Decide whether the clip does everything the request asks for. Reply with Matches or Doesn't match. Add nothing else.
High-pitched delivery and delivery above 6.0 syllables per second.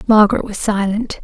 Doesn't match